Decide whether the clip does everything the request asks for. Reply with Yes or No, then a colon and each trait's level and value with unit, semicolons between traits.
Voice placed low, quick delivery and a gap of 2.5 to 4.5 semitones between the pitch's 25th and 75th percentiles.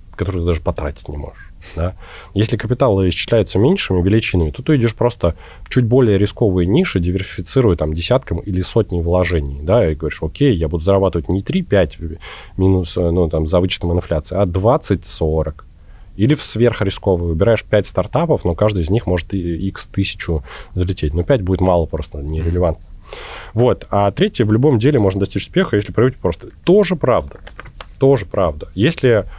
No: very low, 95 Hz; fast, 165 wpm; average, 5.1 semitones